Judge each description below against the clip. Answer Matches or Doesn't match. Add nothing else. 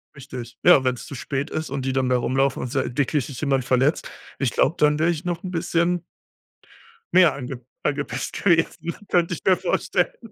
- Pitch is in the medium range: Matches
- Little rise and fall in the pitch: Doesn't match